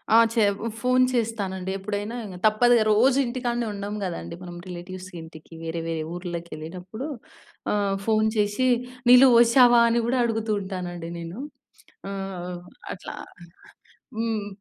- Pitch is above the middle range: Yes, high, 205 Hz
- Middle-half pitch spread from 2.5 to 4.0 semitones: No, average, 4.5 semitones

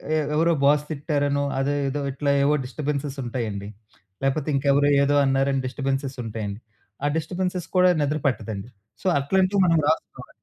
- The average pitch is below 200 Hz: Yes, medium, 140 Hz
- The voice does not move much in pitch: Yes, narrow, 2.3 semitones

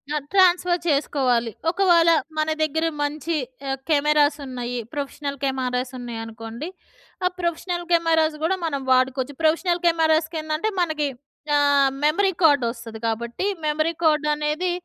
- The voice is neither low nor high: No, very high, 300 Hz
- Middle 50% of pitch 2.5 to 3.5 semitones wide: No, average, 3.9 semitones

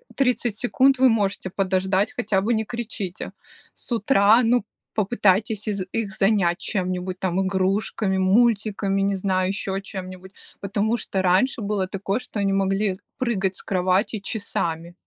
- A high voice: Yes, high, 195 Hz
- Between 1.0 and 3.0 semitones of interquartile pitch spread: Yes, average, 2.7 semitones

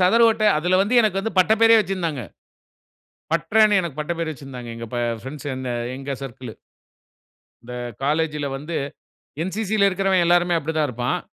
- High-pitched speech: No, medium, 165 Hz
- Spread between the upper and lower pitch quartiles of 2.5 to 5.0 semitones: No, wide, 5.4 semitones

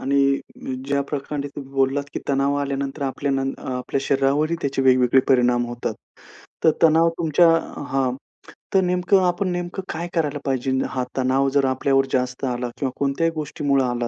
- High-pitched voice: No, medium, 140 Hz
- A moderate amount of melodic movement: No, narrow, 2.3 semitones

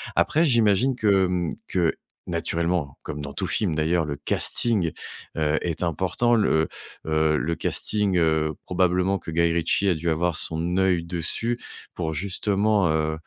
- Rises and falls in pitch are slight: No, average, 3.6 semitones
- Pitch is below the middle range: Yes, very low, 85 Hz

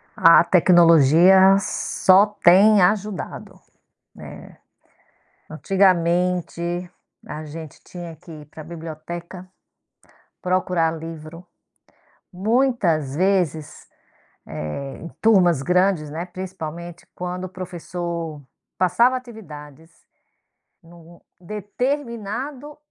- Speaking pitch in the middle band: Yes, medium, 175 Hz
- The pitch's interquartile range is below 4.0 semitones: Yes, average, 2.9 semitones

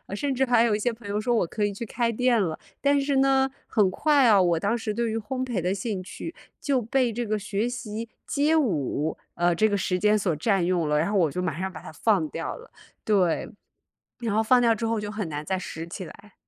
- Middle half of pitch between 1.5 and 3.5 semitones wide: No, average, 4.6 semitones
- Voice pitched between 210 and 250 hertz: Yes, high, 215 Hz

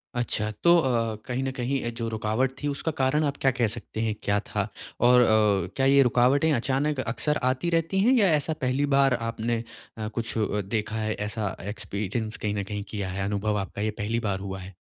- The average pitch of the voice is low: Yes, low, 115 Hz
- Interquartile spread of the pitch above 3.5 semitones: Yes, average, 4.1 semitones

